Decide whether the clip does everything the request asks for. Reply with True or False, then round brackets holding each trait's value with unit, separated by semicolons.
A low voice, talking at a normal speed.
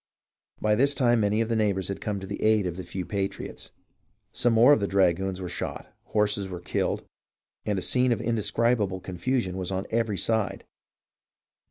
True (105 Hz; 190 wpm)